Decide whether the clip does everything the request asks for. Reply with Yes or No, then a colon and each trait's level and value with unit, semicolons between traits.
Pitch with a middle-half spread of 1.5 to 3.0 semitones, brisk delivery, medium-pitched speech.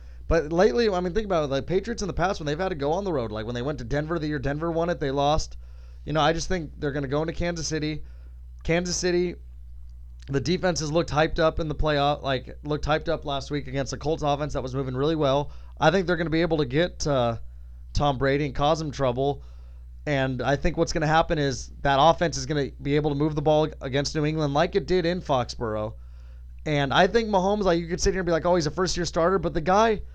No: average, 4.0 semitones; fast, 270 wpm; medium, 150 Hz